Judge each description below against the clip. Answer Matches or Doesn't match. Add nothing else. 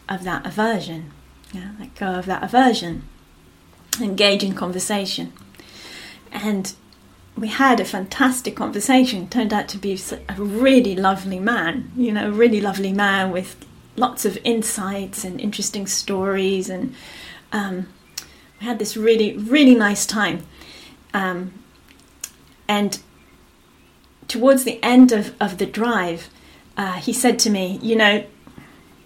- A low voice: Doesn't match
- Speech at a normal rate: Doesn't match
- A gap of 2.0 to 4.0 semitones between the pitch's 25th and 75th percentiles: Matches